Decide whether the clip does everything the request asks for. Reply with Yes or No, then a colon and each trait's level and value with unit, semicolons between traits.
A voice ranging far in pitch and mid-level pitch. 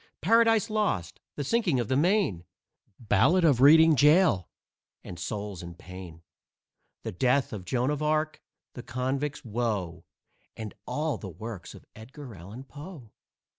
No: wide, 7.5 semitones; low, 125 Hz